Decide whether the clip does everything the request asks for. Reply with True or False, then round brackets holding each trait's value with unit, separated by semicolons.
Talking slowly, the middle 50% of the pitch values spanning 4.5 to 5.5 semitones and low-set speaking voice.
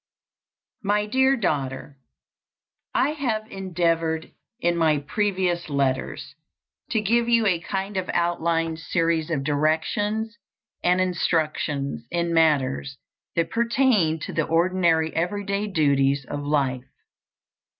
False (115 wpm; 4.9 semitones; 170 Hz)